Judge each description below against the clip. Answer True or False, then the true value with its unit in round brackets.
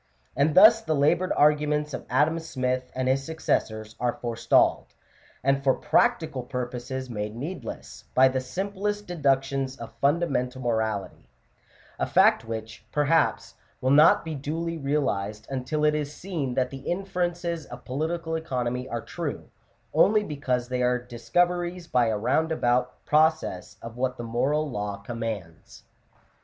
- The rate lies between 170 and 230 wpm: False (145 wpm)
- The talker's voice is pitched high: False (135 Hz)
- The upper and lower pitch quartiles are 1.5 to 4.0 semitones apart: False (4.6 semitones)